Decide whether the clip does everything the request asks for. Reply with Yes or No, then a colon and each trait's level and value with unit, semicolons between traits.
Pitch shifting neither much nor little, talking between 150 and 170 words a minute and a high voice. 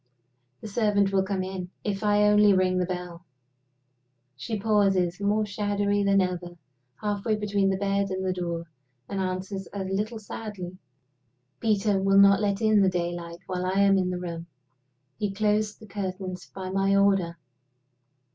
No: narrow, 1.9 semitones; average, 160 wpm; high, 195 Hz